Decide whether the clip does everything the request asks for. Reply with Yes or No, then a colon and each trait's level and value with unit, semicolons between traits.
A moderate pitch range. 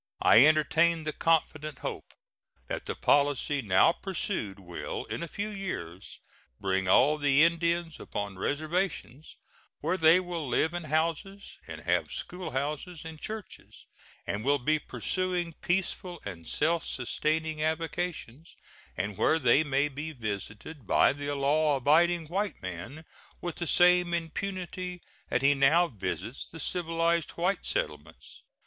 Yes: average, 3.9 semitones